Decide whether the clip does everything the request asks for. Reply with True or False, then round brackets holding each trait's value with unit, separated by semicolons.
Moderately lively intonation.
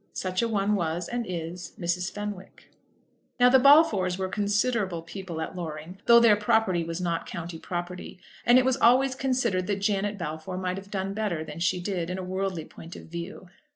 True (3.3 semitones)